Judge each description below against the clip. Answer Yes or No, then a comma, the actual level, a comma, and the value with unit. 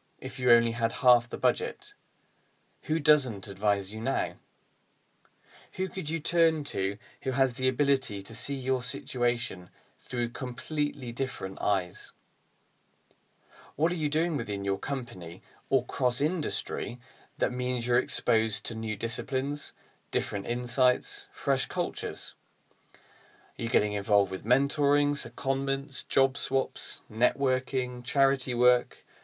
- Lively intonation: No, average, 3.3 semitones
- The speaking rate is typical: No, slow, 125 wpm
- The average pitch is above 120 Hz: Yes, low, 130 Hz